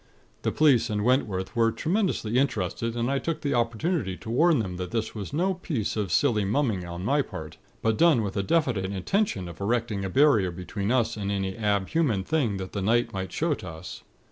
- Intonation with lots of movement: Yes, wide, 6.2 semitones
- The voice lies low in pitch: Yes, low, 110 Hz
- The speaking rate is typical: No, fast, 210 wpm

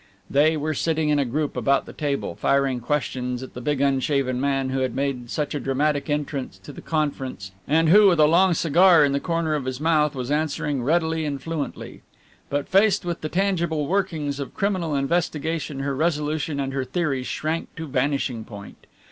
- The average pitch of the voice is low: No, medium, 145 Hz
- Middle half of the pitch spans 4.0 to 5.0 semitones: No, average, 2.9 semitones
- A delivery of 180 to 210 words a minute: Yes, average, 190 wpm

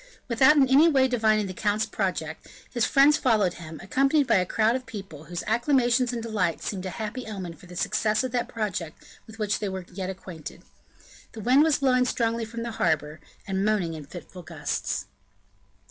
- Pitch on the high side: Yes, high, 215 Hz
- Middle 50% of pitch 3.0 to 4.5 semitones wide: No, average, 5.1 semitones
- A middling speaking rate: Yes, average, 190 wpm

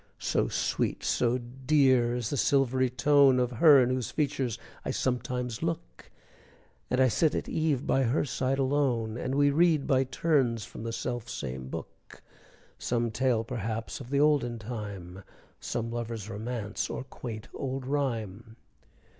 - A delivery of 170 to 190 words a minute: No, average, 155 wpm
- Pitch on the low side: Yes, low, 125 Hz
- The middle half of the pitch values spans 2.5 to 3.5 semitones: Yes, average, 2.9 semitones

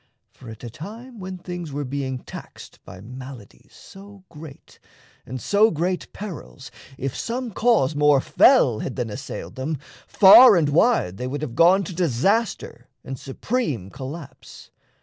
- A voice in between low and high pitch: Yes, medium, 150 Hz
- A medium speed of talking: Yes, average, 150 wpm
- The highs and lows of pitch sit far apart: Yes, wide, 7.1 semitones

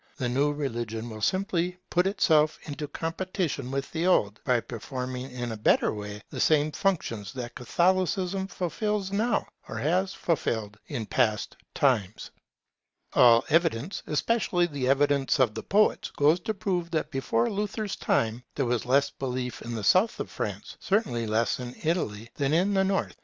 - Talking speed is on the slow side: No, average, 165 wpm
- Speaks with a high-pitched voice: No, medium, 145 Hz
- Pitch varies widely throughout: Yes, wide, 7.3 semitones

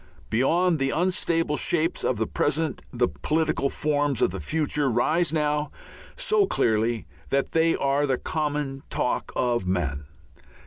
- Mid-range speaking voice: Yes, medium, 145 Hz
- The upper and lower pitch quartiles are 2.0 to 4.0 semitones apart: No, average, 4.6 semitones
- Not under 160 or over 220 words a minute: No, average, 140 wpm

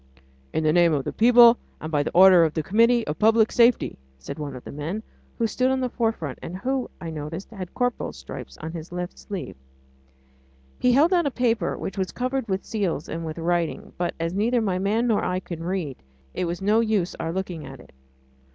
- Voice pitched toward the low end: No, high, 190 Hz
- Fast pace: Yes, fast, 220 wpm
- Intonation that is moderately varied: No, wide, 5.9 semitones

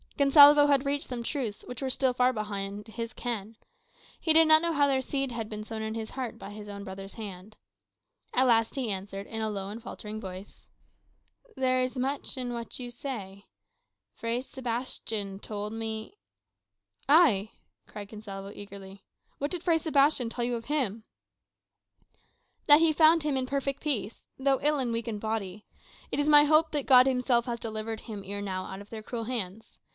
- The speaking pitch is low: No, high, 230 Hz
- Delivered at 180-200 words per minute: Yes, average, 190 wpm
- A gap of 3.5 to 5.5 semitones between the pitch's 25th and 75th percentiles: Yes, average, 4.6 semitones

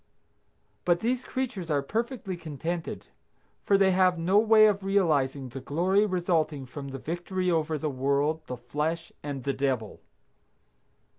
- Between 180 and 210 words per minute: No, average, 145 wpm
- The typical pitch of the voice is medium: Yes, medium, 165 Hz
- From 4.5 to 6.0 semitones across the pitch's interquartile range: Yes, average, 5.2 semitones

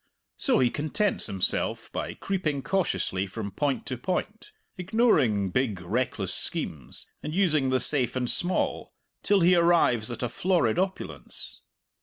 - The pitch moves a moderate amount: No, wide, 7.8 semitones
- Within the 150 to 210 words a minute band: No, average, 140 wpm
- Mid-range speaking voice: Yes, medium, 145 Hz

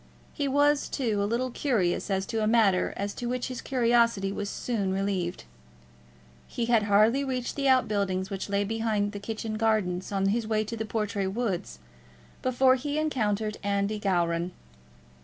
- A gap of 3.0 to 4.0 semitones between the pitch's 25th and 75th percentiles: Yes, average, 3.3 semitones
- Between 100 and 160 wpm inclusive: No, average, 170 wpm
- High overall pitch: Yes, high, 215 Hz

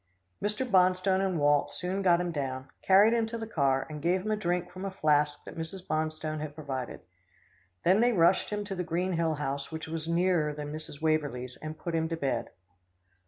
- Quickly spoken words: Yes, fast, 210 wpm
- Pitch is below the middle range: No, medium, 165 Hz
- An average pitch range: Yes, average, 3.9 semitones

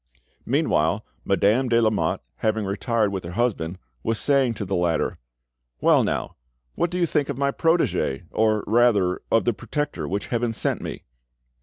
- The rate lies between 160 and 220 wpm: Yes, average, 165 wpm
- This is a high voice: No, low, 110 Hz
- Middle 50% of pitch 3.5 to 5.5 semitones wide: Yes, average, 4.5 semitones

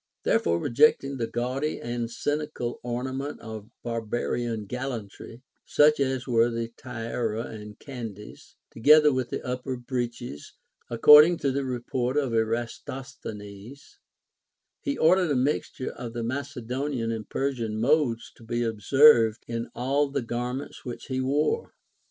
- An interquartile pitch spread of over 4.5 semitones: No, average, 3.1 semitones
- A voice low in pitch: Yes, low, 125 Hz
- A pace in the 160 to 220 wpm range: No, average, 140 wpm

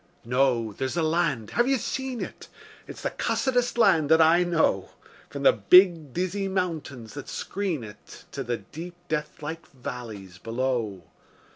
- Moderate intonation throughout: No, wide, 6.6 semitones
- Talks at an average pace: Yes, average, 150 wpm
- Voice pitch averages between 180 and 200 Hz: No, medium, 155 Hz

